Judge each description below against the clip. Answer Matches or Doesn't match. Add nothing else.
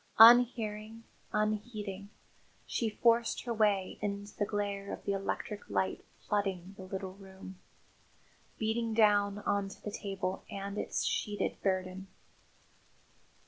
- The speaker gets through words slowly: Matches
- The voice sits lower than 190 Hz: Doesn't match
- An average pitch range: Doesn't match